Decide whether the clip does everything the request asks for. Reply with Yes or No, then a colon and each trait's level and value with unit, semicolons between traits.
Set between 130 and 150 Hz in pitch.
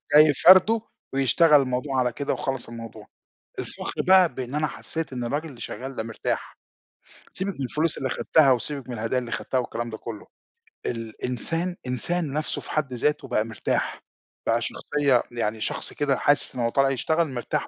Yes: low, 135 Hz